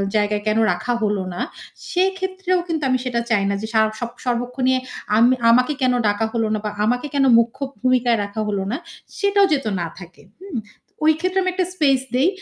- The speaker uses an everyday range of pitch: No, wide, 6.6 semitones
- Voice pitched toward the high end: Yes, very high, 250 Hz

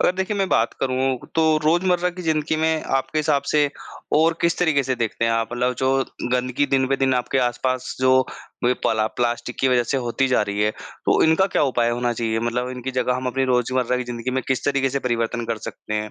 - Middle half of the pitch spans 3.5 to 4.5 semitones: No, average, 3.1 semitones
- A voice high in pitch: No, low, 130 Hz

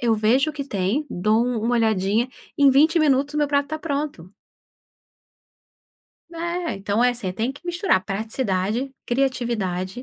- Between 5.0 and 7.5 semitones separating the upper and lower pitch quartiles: Yes, average, 5.3 semitones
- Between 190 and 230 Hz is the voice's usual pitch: No, high, 245 Hz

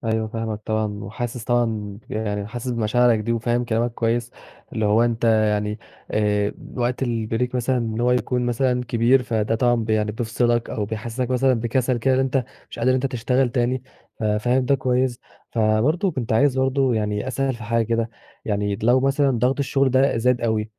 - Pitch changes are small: Yes, narrow, 2.3 semitones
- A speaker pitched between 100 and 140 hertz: Yes, low, 120 Hz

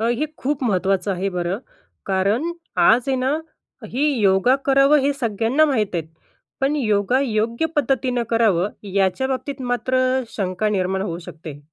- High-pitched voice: Yes, high, 225 Hz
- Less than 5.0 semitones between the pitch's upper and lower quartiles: No, wide, 5.6 semitones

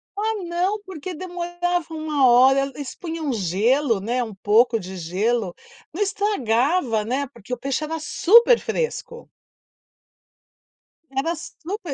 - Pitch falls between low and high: No, very high, 285 Hz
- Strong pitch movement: Yes, wide, 7.0 semitones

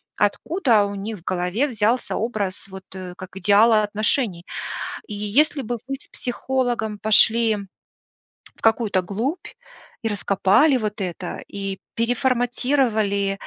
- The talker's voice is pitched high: Yes, high, 215 Hz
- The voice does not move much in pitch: No, average, 3.7 semitones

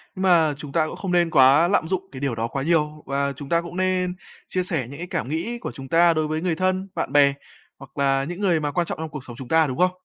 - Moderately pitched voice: Yes, medium, 160 Hz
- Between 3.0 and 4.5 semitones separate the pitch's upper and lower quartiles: Yes, average, 4.1 semitones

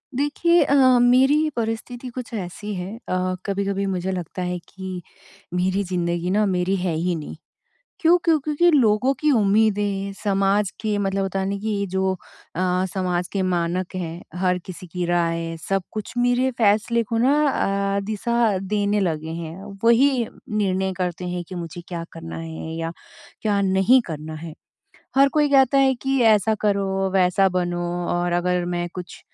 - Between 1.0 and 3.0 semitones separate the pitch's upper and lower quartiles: No, average, 3.8 semitones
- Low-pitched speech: No, high, 195 Hz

